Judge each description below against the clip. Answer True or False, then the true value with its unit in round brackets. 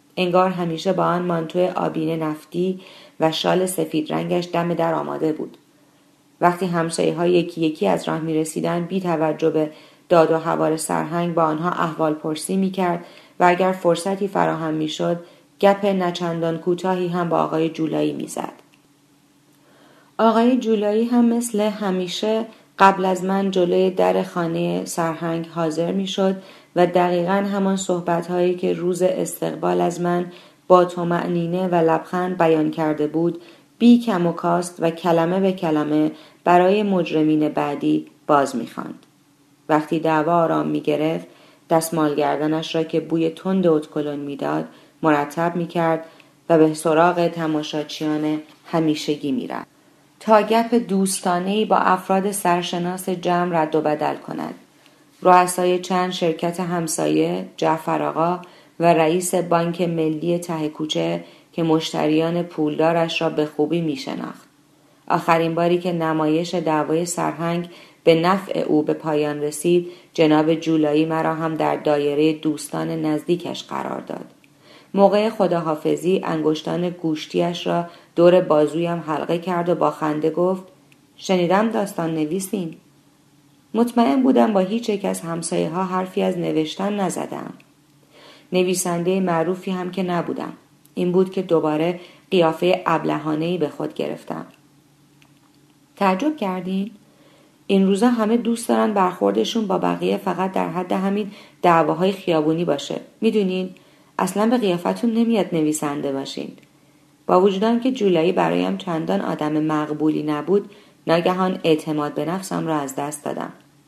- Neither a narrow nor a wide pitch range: True (3.0 semitones)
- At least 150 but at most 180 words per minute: False (135 wpm)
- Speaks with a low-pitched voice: False (170 Hz)